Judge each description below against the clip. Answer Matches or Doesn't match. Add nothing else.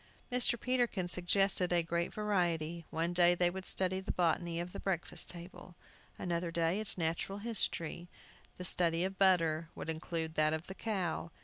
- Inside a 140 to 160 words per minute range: Doesn't match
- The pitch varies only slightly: Matches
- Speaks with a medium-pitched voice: Matches